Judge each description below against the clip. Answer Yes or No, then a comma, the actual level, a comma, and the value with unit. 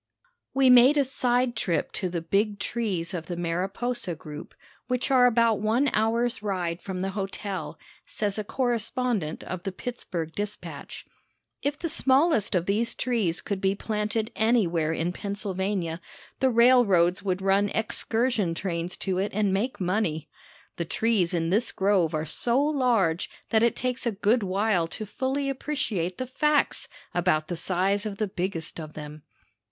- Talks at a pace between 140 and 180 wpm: Yes, average, 160 wpm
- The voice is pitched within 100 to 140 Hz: No, high, 205 Hz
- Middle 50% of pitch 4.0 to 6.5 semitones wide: Yes, average, 5.1 semitones